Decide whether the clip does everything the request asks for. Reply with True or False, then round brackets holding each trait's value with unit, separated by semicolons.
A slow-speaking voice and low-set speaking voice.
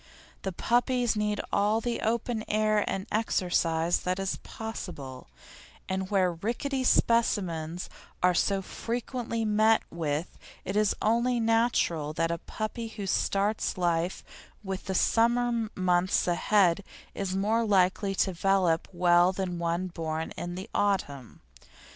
False (130 wpm; 195 Hz)